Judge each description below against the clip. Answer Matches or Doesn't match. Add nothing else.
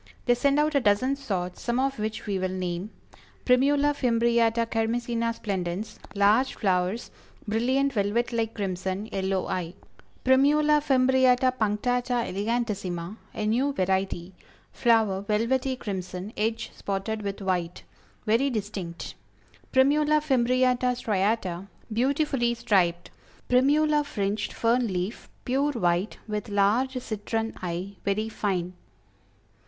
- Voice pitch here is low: Doesn't match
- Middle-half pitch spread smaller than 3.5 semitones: Doesn't match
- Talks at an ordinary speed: Doesn't match